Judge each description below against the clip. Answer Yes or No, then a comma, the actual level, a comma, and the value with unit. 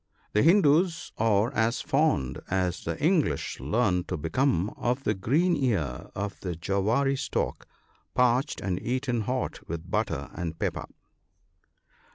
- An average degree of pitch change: No, wide, 7.0 semitones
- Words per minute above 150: No, average, 140 wpm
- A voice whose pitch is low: Yes, low, 115 Hz